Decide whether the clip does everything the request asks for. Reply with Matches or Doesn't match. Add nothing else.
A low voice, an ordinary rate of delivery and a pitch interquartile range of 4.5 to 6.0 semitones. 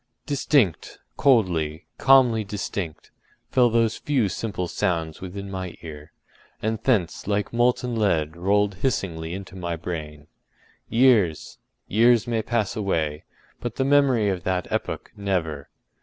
Doesn't match